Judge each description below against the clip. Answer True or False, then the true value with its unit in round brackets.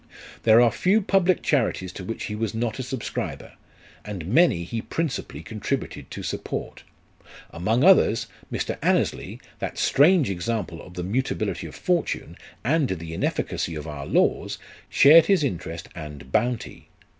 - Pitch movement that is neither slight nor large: False (8.6 semitones)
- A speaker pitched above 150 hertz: False (115 Hz)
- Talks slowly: False (145 wpm)